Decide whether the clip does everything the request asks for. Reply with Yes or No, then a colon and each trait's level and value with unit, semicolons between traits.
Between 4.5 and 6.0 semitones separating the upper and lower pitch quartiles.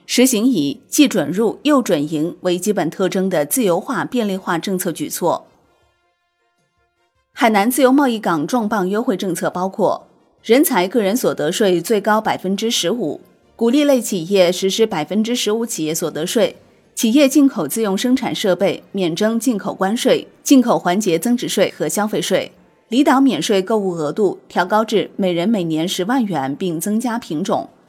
Yes: wide, 5.4 semitones